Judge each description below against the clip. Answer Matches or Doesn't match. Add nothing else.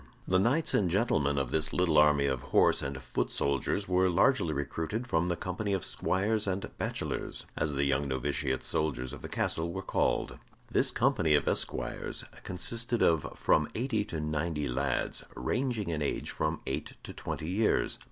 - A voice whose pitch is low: Matches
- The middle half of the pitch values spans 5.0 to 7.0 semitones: Matches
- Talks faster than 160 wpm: Matches